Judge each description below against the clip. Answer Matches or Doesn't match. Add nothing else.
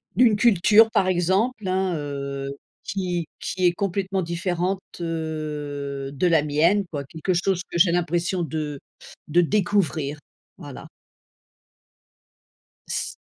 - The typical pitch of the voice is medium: Matches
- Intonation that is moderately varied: Matches